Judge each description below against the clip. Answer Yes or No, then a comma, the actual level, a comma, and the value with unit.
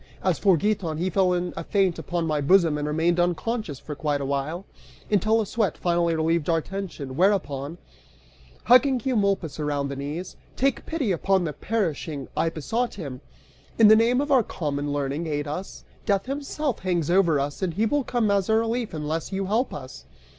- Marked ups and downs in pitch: Yes, wide, 5.8 semitones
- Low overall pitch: No, medium, 175 Hz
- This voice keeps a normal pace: Yes, average, 190 wpm